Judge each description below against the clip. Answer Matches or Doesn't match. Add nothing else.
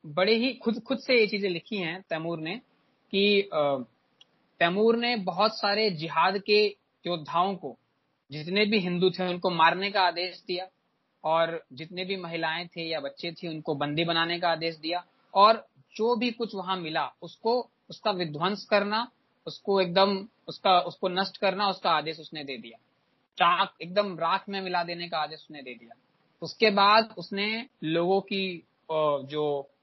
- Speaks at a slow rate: Doesn't match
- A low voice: Doesn't match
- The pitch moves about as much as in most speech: Matches